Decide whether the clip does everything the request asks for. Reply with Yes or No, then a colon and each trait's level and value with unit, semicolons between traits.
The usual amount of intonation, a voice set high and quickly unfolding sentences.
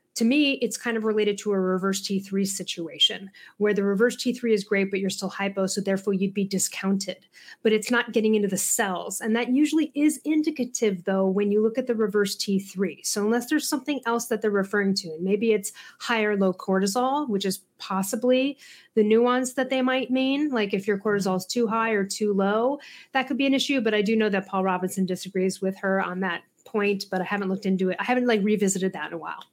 Yes: average, 3.7 semitones; high, 210 Hz; fast, 230 wpm